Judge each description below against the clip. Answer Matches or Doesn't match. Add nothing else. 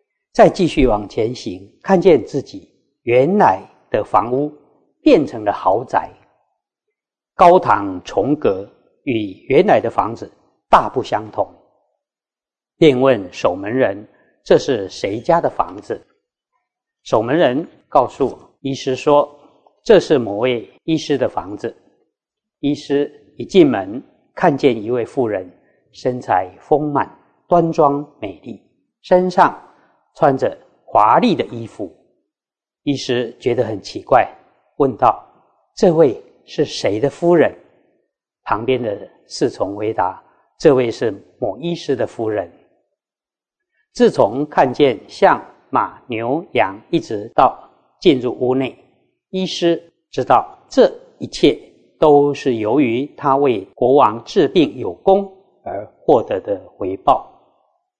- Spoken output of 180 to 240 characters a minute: Doesn't match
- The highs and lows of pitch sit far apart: Matches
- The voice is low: Doesn't match